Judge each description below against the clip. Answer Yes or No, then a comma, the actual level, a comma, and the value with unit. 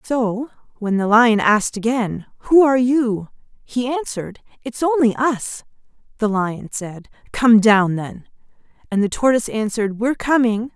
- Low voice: No, high, 230 Hz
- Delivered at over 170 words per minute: No, average, 145 wpm